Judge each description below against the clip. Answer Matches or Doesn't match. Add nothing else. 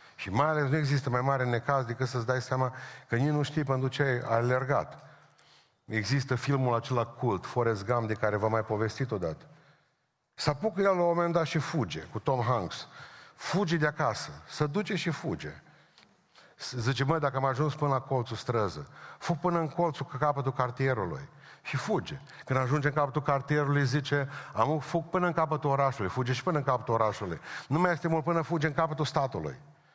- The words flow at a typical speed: Doesn't match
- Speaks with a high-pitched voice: Doesn't match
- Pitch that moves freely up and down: Doesn't match